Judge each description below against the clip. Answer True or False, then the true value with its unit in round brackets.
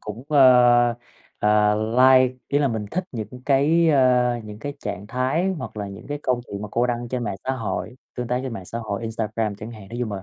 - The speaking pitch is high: False (120 Hz)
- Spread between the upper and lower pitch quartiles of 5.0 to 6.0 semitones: False (3.4 semitones)